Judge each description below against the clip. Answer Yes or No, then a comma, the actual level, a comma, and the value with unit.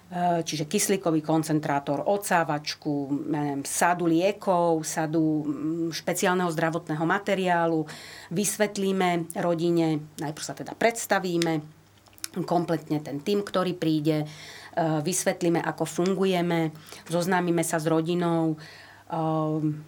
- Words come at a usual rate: No, slow, 85 wpm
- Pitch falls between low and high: Yes, medium, 165 Hz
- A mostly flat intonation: Yes, narrow, 2.3 semitones